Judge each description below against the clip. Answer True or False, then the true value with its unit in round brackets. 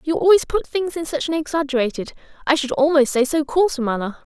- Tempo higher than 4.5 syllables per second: True (6.3 syllables/s)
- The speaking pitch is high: True (300 Hz)